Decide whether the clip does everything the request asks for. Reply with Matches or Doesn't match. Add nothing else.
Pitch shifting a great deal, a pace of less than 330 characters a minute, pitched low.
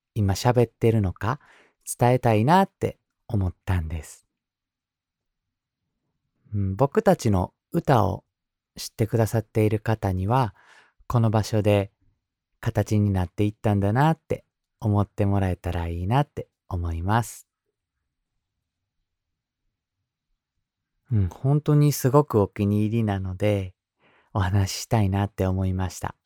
Doesn't match